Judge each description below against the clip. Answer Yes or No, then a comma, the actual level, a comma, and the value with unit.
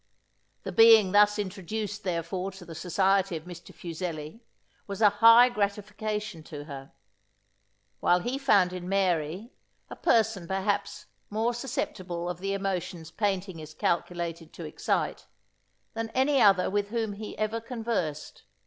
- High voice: Yes, high, 195 Hz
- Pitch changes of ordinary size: Yes, average, 3.7 semitones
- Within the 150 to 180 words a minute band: No, average, 140 wpm